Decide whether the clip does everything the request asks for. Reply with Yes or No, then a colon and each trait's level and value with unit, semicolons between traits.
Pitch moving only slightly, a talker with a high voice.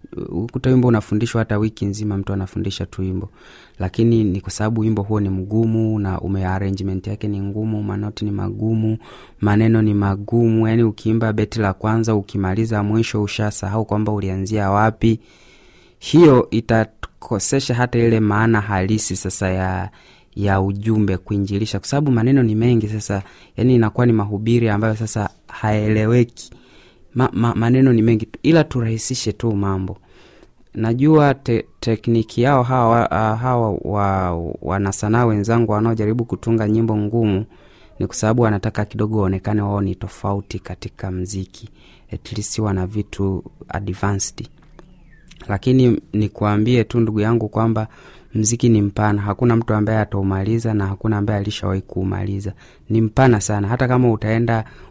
No: narrow, 2.3 semitones; low, 110 Hz